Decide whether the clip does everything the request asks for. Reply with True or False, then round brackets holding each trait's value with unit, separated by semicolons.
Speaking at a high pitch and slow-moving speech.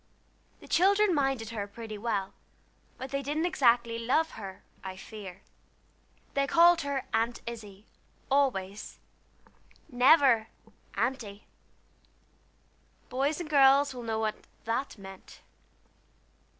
True (240 Hz; 110 wpm)